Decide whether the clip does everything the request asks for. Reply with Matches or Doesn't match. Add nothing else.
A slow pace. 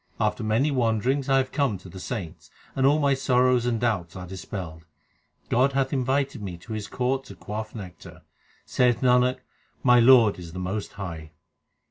Doesn't match